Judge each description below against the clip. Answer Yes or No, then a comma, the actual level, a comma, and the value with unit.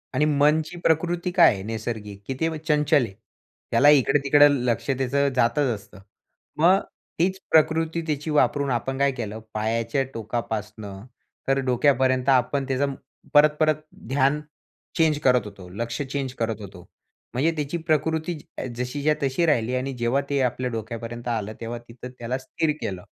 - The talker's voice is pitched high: No, low, 135 Hz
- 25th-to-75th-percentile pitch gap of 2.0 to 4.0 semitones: No, average, 4.4 semitones